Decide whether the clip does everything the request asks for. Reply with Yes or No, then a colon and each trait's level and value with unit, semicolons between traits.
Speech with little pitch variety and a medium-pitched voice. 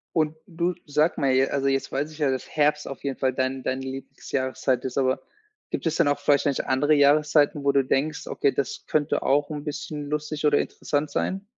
Yes: narrow, 2.0 semitones; medium, 145 Hz